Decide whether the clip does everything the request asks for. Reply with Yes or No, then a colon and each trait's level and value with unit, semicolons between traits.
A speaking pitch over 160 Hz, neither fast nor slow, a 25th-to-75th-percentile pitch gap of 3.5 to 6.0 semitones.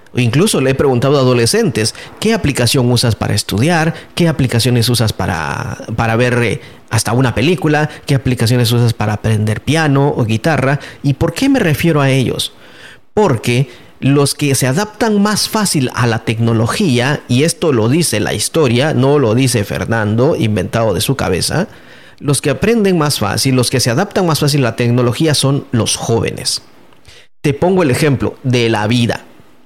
No: low, 125 Hz; average, 170 wpm; average, 4.4 semitones